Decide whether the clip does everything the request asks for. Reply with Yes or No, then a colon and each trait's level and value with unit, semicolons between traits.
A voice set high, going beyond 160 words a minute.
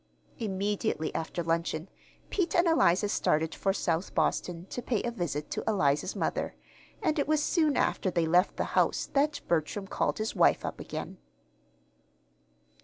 No: high, 195 Hz; average, 155 wpm